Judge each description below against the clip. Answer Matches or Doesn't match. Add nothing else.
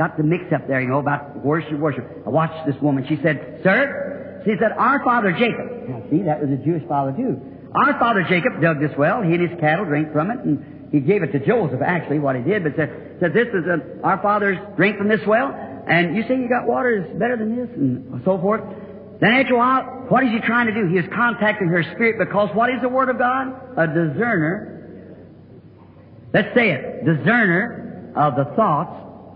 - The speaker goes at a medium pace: Doesn't match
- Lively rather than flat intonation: Matches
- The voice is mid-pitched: Matches